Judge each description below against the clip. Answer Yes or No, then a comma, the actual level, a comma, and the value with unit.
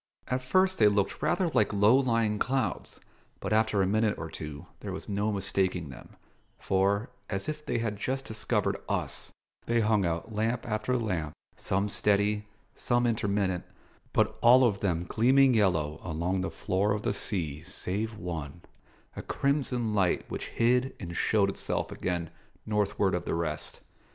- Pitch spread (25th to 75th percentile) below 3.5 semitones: No, average, 4.0 semitones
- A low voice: Yes, low, 105 Hz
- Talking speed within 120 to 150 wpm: No, average, 160 wpm